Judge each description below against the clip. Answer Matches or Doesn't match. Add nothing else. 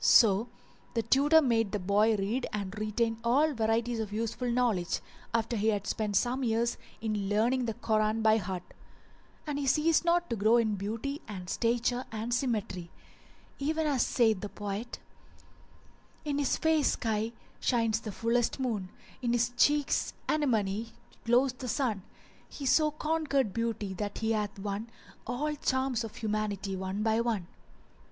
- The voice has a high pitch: Matches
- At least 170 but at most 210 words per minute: Doesn't match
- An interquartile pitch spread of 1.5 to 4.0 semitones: Matches